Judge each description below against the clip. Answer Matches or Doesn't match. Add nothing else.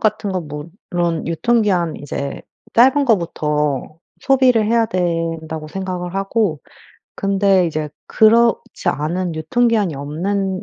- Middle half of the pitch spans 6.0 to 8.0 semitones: Doesn't match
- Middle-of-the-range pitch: Matches